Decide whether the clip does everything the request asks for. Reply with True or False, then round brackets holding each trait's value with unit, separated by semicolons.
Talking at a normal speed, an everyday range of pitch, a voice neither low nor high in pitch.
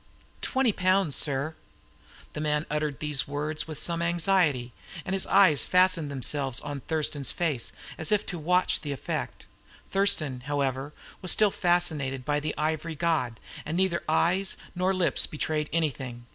True (150 wpm; 3.7 semitones; 155 Hz)